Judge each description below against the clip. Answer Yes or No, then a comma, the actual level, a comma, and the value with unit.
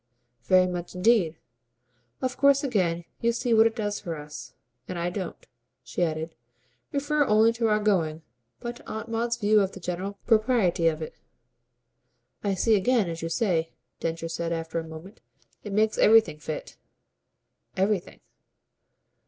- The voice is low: No, high, 195 Hz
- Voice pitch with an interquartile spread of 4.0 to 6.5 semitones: Yes, average, 5.2 semitones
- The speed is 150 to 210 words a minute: Yes, average, 155 wpm